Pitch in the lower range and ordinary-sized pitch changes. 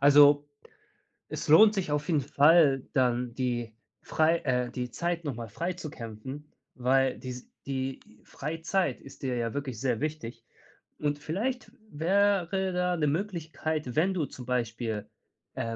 No: medium, 145 Hz; average, 4.9 semitones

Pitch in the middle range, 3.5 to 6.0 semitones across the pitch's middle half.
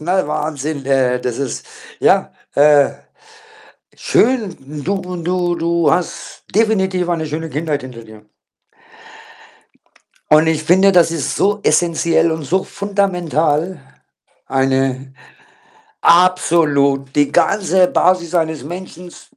Yes: medium, 165 Hz; average, 4.1 semitones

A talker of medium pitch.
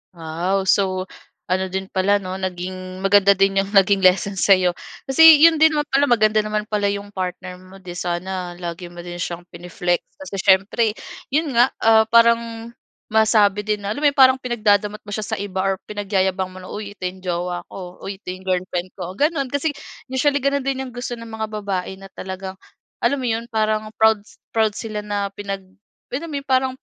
No: high, 200 Hz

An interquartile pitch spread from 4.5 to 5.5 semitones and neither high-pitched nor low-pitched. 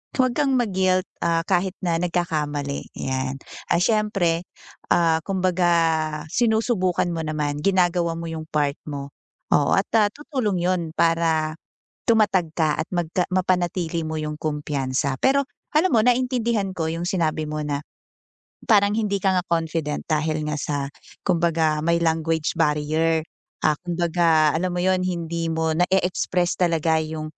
No: average, 2.9 semitones; medium, 170 Hz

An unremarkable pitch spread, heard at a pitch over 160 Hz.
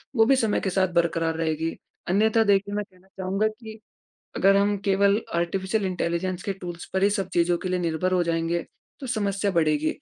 Yes: average, 3.0 semitones; high, 190 Hz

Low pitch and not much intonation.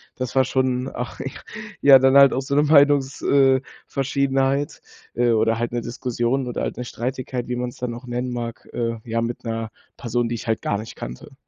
Yes: low, 125 Hz; narrow, 2.2 semitones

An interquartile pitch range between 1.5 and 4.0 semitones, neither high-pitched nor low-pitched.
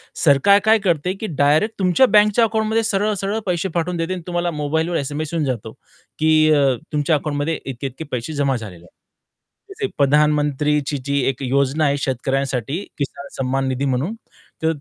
No: average, 4.6 semitones; medium, 150 Hz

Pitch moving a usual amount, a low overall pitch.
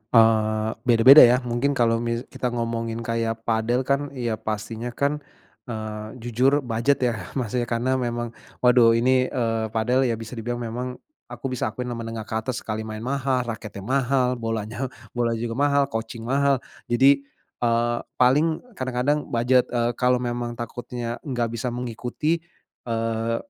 No: narrow, 1.9 semitones; low, 120 Hz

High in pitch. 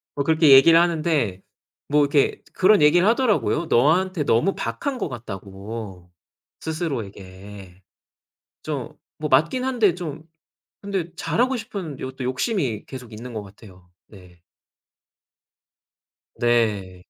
No: low, 135 Hz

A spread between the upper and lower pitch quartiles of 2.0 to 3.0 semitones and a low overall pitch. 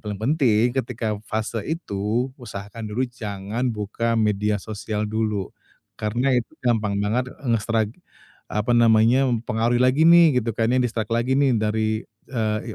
Yes: narrow, 2.5 semitones; low, 115 Hz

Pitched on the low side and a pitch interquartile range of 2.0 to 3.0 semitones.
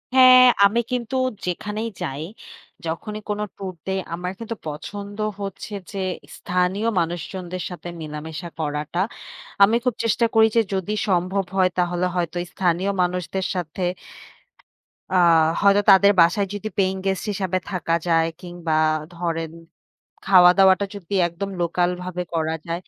No: medium, 185 Hz; average, 2.7 semitones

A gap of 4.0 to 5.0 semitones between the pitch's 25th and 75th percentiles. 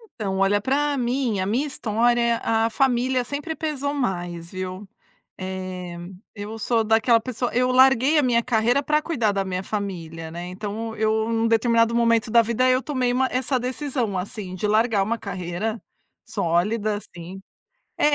Yes: average, 4.4 semitones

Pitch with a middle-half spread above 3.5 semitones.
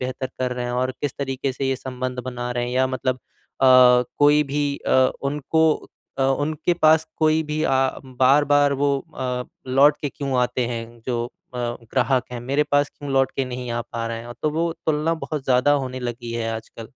No: average, 2.7 semitones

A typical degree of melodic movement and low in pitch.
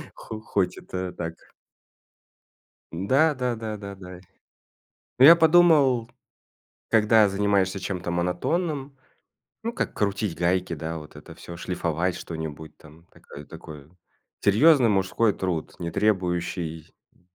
Yes: average, 4.9 semitones; very low, 95 Hz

